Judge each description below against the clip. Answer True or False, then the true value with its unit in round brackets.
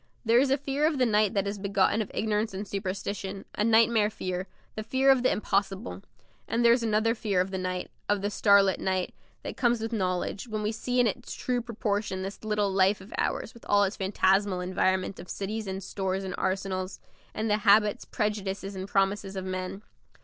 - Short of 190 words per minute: False (205 wpm)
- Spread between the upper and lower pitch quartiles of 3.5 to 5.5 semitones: False (2.6 semitones)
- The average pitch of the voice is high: True (205 Hz)